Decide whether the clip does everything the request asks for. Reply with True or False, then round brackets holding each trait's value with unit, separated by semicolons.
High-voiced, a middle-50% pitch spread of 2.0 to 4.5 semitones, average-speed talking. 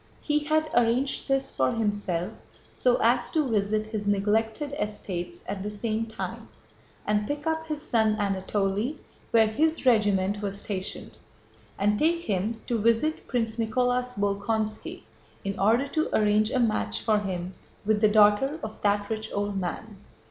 True (215 Hz; 3.3 semitones; 155 wpm)